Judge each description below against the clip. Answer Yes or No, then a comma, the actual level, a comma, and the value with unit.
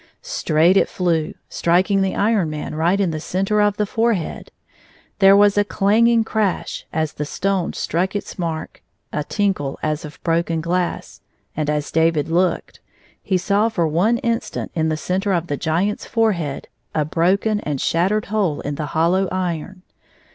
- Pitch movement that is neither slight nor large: Yes, average, 4.2 semitones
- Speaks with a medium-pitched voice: Yes, medium, 180 Hz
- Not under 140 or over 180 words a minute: Yes, average, 170 wpm